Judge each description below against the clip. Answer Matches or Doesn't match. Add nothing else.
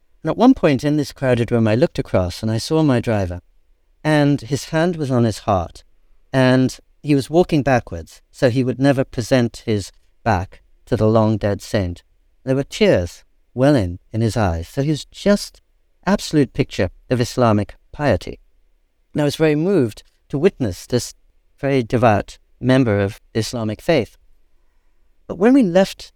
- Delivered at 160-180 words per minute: Matches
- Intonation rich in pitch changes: Matches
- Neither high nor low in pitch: Doesn't match